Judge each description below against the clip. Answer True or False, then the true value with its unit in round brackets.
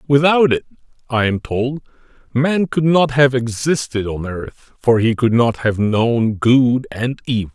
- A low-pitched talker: True (125 Hz)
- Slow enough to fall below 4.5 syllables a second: True (4.0 syllables/s)